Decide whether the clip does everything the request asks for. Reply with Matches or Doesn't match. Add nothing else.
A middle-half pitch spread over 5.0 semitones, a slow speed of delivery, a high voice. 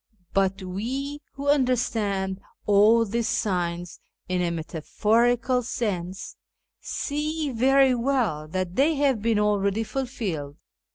Matches